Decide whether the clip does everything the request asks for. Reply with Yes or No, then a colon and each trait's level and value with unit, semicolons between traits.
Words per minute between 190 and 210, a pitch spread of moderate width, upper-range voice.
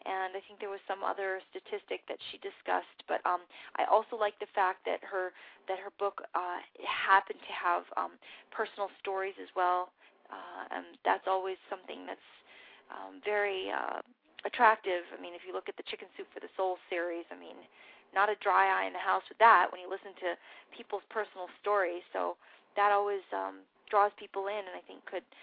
No: average, 200 wpm; narrow, 2.3 semitones; high, 195 Hz